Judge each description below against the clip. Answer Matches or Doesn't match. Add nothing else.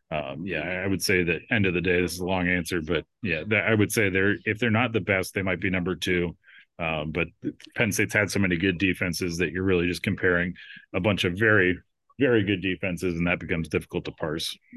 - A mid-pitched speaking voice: Doesn't match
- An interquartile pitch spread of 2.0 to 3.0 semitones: Matches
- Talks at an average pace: Doesn't match